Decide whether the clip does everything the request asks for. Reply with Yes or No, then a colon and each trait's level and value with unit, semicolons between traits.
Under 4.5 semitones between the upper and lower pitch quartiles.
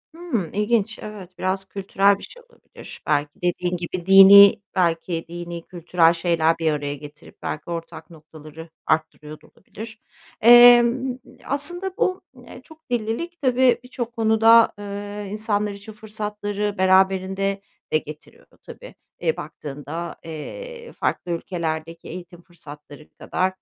No: average, 5.3 semitones